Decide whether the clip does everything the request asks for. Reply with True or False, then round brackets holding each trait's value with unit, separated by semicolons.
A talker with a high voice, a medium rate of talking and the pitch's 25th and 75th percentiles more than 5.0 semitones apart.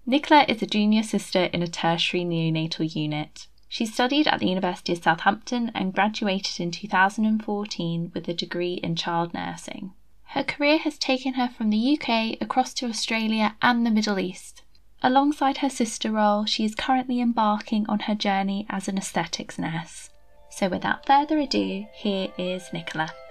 True (210 Hz; 165 wpm; 5.5 semitones)